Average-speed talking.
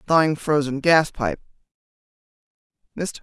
No: slow, 75 wpm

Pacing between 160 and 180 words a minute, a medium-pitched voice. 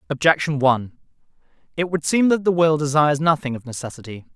Yes: average, 165 wpm; medium, 150 Hz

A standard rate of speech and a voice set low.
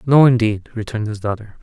Yes: average, 185 wpm; low, 110 Hz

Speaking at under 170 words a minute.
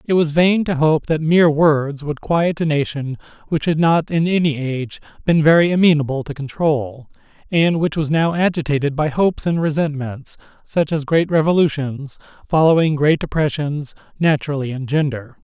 Yes: average, 160 wpm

